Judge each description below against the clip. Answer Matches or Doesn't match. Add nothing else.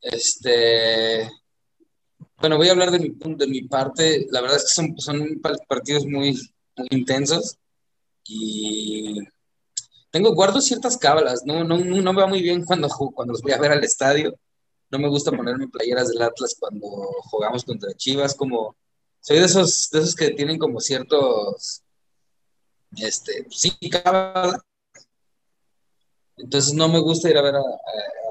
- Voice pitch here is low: Doesn't match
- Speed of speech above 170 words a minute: Doesn't match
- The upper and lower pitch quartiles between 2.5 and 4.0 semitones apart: Doesn't match